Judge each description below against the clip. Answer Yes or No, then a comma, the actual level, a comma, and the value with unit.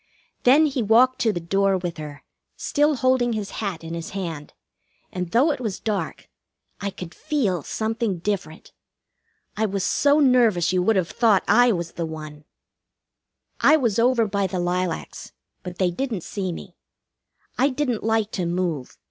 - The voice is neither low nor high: No, high, 200 Hz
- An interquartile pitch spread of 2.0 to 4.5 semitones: No, wide, 5.4 semitones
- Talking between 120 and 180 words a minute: Yes, average, 165 wpm